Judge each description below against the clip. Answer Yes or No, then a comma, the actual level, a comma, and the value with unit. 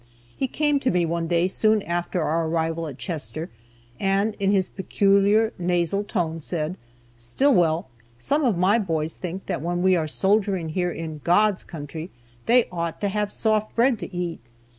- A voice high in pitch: No, medium, 180 Hz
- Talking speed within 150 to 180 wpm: Yes, average, 170 wpm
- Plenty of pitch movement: No, average, 3.9 semitones